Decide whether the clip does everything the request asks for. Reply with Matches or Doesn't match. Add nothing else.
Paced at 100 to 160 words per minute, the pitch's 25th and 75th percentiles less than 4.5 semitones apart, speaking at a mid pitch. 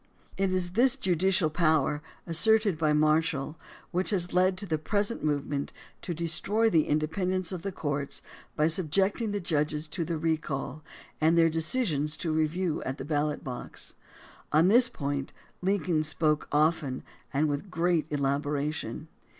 Matches